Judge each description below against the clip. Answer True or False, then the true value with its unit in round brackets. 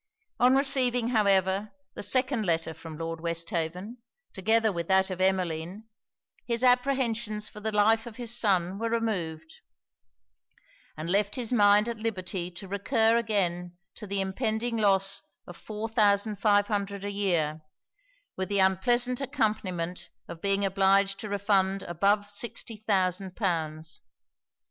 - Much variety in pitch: False (3.4 semitones)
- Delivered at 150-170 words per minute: False (140 wpm)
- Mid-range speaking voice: False (200 Hz)